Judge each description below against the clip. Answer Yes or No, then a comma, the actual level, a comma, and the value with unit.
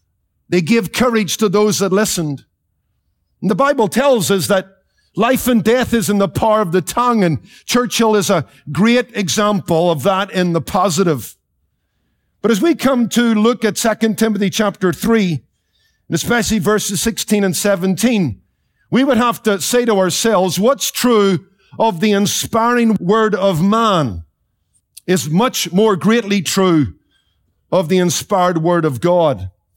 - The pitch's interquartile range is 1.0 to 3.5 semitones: No, average, 4.1 semitones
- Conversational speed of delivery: Yes, average, 155 wpm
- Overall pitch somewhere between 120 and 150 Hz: No, high, 200 Hz